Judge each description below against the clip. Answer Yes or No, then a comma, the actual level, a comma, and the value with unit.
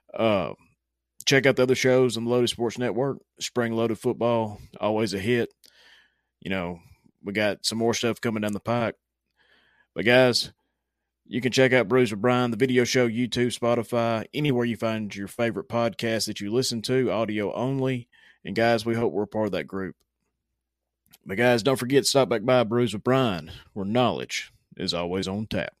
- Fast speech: No, average, 185 wpm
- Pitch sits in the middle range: No, low, 115 Hz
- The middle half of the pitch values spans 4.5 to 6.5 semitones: No, average, 2.7 semitones